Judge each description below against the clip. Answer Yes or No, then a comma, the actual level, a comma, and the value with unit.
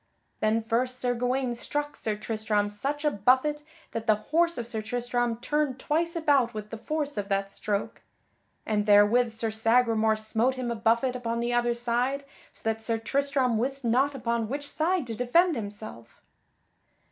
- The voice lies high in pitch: Yes, high, 240 Hz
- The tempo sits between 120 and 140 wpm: No, average, 170 wpm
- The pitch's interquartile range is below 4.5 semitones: Yes, average, 3.6 semitones